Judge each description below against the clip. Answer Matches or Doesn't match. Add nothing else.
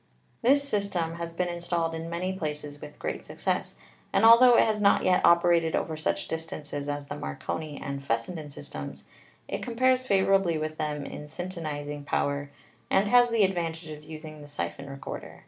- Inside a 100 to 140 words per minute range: Doesn't match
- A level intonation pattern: Doesn't match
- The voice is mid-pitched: Matches